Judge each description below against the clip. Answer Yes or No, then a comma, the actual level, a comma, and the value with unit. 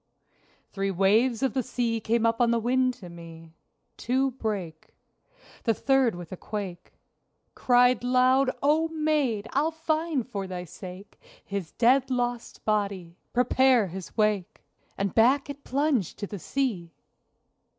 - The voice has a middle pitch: No, high, 230 Hz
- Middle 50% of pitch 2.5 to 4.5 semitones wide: No, average, 5.0 semitones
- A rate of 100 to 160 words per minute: Yes, average, 140 wpm